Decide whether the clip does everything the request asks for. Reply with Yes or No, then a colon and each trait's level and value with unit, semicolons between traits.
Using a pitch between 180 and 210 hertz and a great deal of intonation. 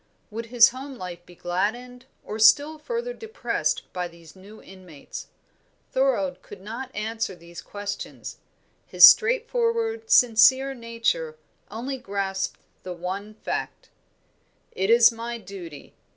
No: high, 225 Hz; wide, 6.0 semitones